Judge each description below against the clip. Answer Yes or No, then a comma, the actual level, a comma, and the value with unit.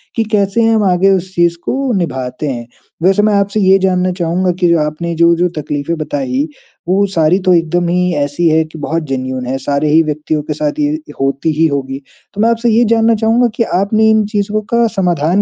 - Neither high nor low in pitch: Yes, medium, 175 Hz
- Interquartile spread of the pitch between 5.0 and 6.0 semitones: Yes, average, 5.3 semitones